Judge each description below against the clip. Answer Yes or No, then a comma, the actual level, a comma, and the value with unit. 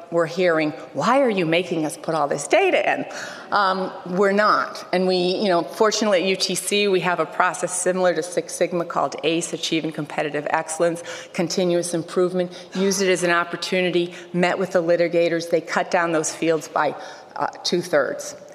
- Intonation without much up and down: Yes, narrow, 1.7 semitones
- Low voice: No, medium, 175 Hz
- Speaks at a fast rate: No, average, 180 wpm